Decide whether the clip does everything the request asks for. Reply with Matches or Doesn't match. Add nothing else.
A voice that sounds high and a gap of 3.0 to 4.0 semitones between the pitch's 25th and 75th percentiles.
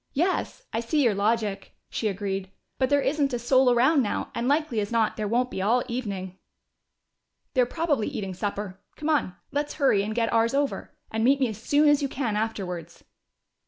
Doesn't match